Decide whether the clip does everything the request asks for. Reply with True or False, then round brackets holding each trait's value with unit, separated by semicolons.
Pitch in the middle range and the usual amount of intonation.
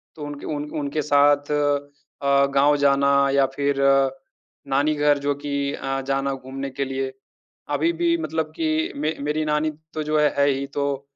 False (145 Hz; 1.4 semitones)